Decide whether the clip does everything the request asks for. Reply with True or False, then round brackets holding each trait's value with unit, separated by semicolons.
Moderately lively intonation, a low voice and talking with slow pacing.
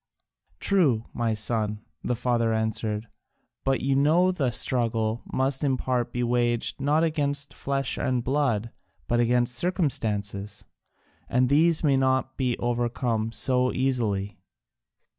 True (3.2 semitones; 125 Hz; 125 wpm)